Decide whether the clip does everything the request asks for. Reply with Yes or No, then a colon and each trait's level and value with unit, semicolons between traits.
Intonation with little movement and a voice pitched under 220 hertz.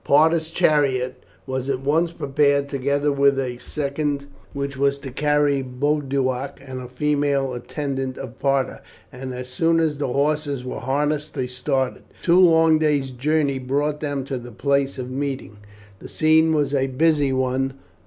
Yes: narrow, 2.2 semitones; medium, 140 Hz